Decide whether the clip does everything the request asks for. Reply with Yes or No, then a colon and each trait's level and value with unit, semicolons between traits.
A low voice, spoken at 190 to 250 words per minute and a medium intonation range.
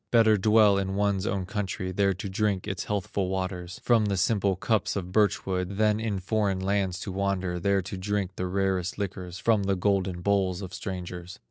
No: very low, 95 Hz; average, 195 wpm; narrow, 1.7 semitones